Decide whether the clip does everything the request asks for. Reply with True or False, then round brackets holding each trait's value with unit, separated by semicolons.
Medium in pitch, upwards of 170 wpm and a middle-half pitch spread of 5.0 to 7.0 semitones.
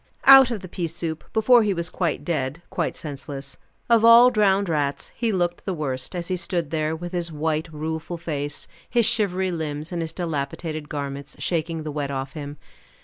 False (165 Hz; 190 wpm; 3.8 semitones)